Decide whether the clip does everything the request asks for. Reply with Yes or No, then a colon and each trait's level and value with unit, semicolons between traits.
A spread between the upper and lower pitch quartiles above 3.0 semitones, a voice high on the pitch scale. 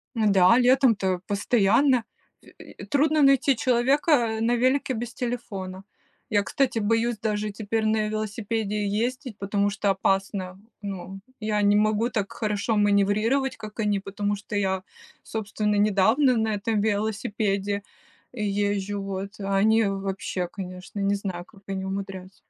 No: narrow, 2.4 semitones; high, 210 Hz